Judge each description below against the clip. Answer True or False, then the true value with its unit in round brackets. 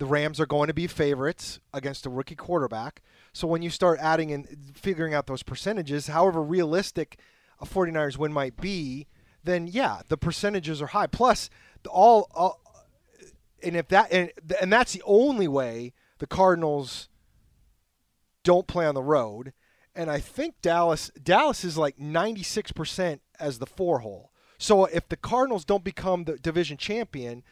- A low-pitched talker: False (165 Hz)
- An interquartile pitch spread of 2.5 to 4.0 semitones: False (4.4 semitones)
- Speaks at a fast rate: False (160 wpm)